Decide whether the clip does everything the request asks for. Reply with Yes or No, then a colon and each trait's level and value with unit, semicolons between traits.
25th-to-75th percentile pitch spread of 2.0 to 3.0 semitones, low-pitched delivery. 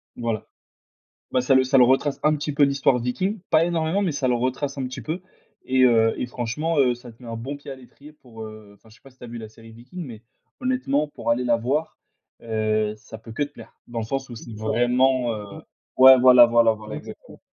No: average, 3.5 semitones; low, 125 Hz